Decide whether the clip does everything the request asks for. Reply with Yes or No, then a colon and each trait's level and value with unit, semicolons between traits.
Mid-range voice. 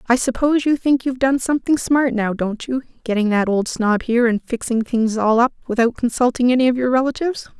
No: high, 245 Hz